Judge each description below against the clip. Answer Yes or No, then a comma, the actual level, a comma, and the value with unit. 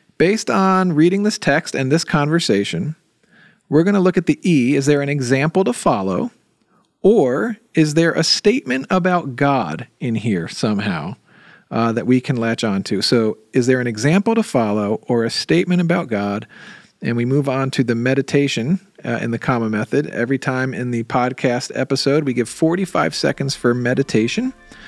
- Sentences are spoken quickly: No, average, 180 wpm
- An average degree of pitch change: No, wide, 6.2 semitones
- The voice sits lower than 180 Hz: Yes, medium, 140 Hz